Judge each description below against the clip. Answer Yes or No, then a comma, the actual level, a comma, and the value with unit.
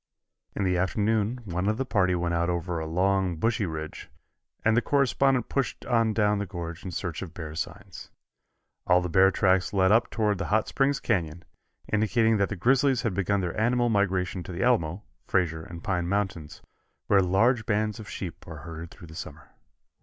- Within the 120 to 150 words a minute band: No, average, 190 wpm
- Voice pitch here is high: No, very low, 95 Hz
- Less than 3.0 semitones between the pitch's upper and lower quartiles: No, average, 4.0 semitones